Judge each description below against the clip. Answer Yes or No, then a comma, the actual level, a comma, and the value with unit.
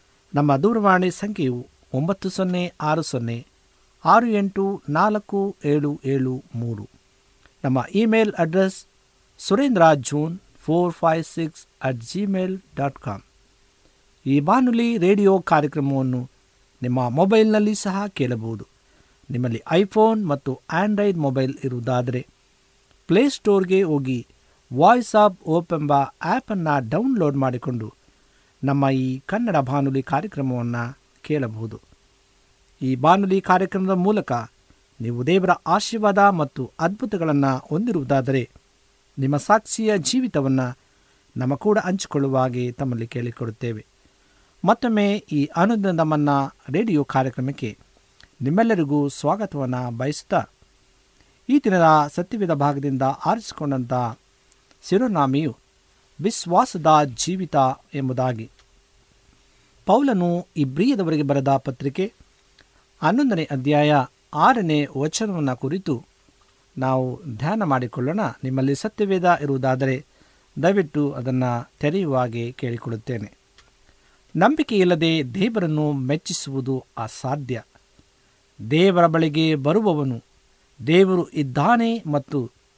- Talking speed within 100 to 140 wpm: No, average, 85 wpm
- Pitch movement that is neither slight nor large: No, wide, 6.6 semitones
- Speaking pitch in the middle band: Yes, medium, 145 Hz